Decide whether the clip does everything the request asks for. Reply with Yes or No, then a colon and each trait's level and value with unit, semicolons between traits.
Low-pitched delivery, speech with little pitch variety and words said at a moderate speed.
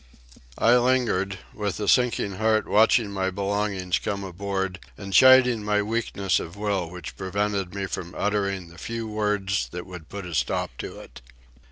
Yes: low, 100 Hz; narrow, 2.0 semitones; average, 165 wpm